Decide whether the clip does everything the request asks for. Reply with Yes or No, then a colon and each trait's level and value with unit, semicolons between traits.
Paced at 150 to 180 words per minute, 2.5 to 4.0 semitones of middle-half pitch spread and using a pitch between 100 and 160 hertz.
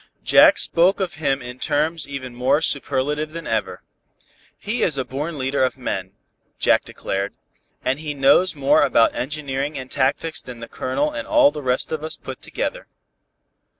Yes: average, 170 wpm; average, 3.3 semitones; medium, 140 Hz